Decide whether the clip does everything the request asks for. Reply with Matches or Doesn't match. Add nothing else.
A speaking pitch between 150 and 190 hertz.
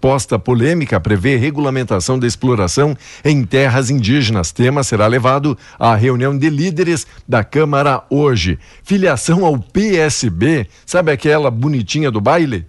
Doesn't match